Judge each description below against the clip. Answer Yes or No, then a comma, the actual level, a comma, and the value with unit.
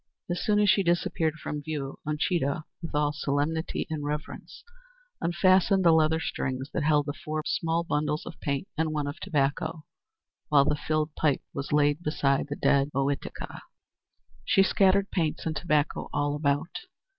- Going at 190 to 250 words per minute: No, average, 160 wpm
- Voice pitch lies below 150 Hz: No, medium, 155 Hz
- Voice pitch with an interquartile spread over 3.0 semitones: No, narrow, 2.4 semitones